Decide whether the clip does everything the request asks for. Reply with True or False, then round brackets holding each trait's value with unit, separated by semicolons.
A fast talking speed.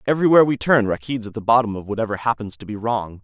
True (240 wpm)